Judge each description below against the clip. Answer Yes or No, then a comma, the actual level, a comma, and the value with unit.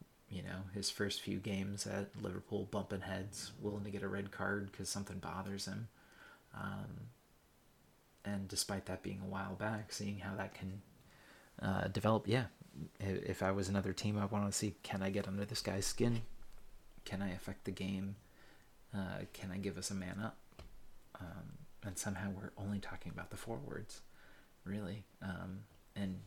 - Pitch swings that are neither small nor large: No, narrow, 1.1 semitones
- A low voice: Yes, low, 100 Hz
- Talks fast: No, average, 175 wpm